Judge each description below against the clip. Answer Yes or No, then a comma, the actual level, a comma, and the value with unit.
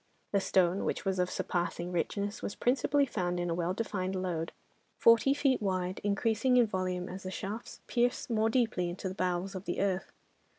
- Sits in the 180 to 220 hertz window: Yes, high, 190 Hz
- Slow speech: No, average, 185 wpm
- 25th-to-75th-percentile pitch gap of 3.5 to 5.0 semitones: Yes, average, 3.8 semitones